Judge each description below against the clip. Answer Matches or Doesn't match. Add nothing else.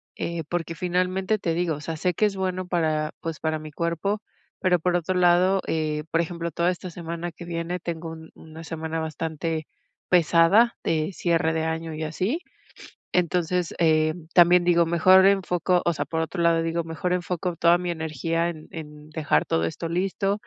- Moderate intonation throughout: Doesn't match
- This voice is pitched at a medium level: Matches